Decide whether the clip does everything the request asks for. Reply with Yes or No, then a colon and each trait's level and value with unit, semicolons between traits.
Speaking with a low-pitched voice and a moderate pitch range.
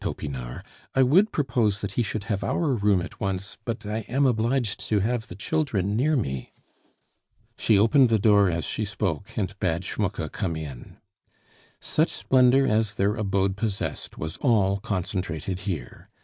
Yes: low, 105 Hz; average, 3.9 semitones